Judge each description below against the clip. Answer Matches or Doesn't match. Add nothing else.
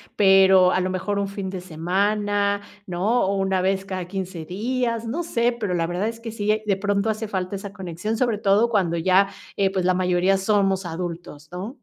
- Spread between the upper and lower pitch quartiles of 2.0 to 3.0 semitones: Matches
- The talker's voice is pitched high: Matches